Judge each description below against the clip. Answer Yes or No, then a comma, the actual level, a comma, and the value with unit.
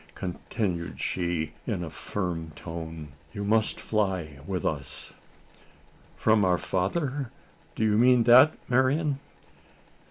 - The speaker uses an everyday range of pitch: No, wide, 5.9 semitones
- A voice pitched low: Yes, low, 100 Hz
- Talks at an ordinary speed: No, slow, 115 wpm